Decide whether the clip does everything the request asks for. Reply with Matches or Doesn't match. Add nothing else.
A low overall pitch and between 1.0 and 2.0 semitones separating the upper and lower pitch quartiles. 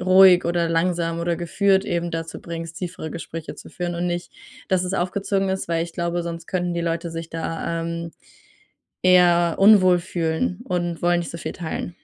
Doesn't match